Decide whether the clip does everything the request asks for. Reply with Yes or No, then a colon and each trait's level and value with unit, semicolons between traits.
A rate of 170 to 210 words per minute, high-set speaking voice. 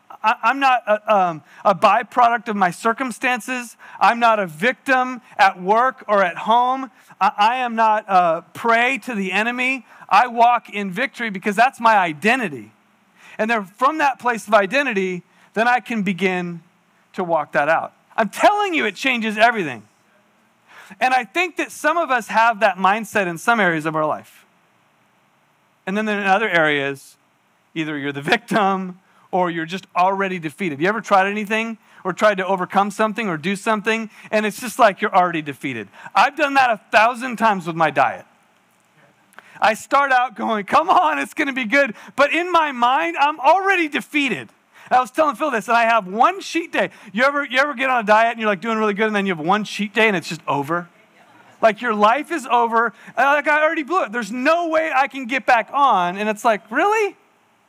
Yes: average, 200 wpm; high, 225 Hz